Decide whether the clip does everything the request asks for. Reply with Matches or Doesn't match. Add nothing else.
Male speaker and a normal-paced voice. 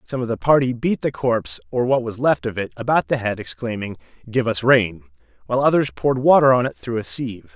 Doesn't match